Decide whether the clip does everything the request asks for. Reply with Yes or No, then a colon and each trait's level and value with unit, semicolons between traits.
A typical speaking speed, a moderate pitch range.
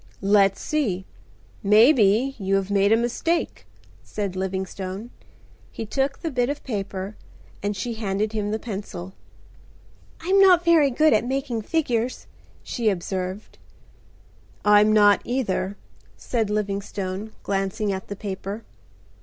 No: slow, 125 wpm; average, 3.9 semitones